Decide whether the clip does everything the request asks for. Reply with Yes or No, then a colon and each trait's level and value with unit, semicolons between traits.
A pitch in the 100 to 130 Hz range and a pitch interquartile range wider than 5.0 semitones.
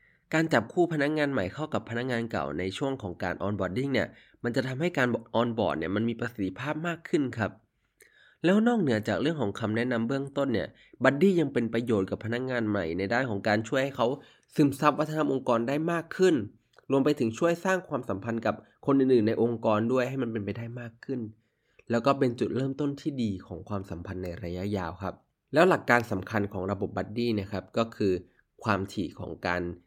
Yes: low, 115 Hz; wide, 5.4 semitones